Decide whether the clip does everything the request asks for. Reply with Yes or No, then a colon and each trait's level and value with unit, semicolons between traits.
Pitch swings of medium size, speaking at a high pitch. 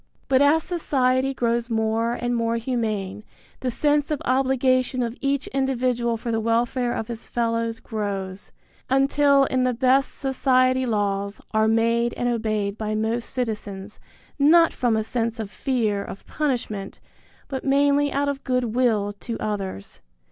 Yes: average, 3.3 semitones; high, 240 Hz